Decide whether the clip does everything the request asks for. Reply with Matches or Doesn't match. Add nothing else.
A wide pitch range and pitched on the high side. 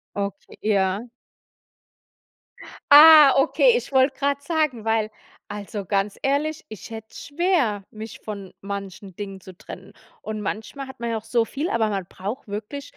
Matches